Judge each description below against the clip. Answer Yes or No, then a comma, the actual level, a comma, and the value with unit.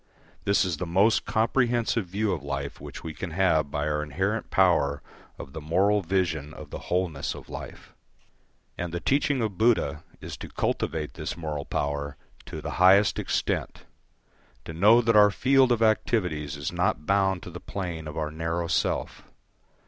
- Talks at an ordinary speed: Yes, average, 170 wpm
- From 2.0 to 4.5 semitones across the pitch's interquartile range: No, average, 5.1 semitones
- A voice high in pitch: No, very low, 90 Hz